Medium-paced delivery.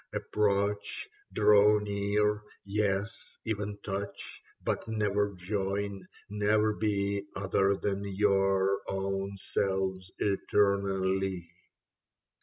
No: slow, 80 wpm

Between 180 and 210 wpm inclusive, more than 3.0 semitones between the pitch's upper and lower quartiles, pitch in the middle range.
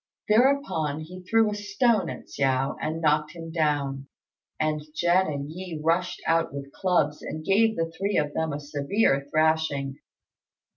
No: average, 155 wpm; average, 4.0 semitones; medium, 160 Hz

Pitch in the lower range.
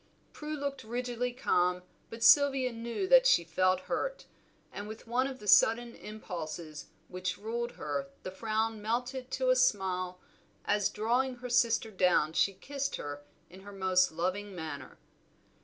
No: high, 220 Hz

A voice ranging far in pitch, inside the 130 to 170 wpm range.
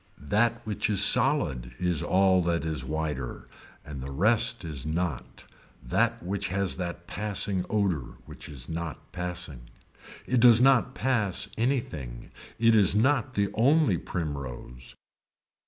Yes: wide, 6.5 semitones; slow, 135 wpm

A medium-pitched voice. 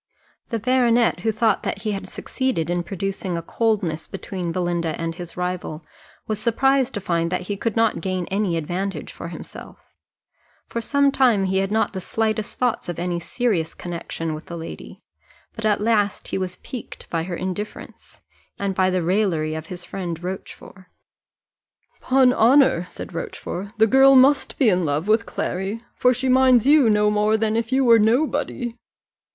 No: high, 205 Hz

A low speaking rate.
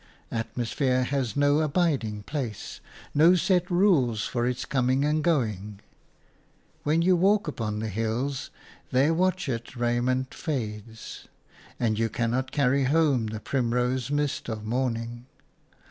Yes: slow, 125 wpm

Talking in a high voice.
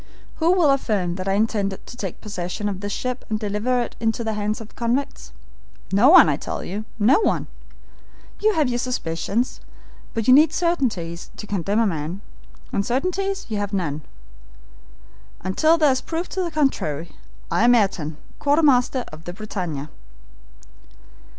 Yes: high, 220 Hz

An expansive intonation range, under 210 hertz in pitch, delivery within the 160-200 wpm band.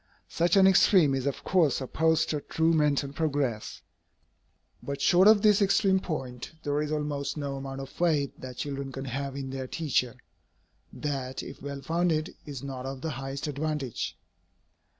No: average, 3.0 semitones; medium, 140 Hz; average, 165 wpm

